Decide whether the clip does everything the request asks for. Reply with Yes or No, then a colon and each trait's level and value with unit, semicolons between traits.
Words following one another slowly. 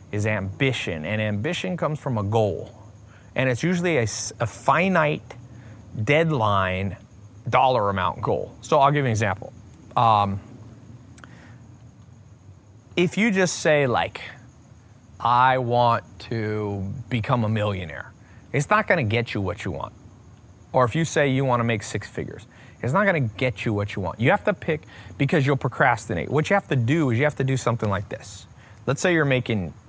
No: average, 175 wpm